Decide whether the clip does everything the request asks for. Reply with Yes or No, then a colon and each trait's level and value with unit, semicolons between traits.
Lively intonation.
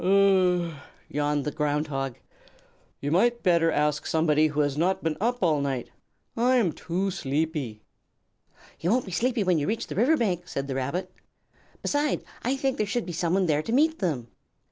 Yes: wide, 6.2 semitones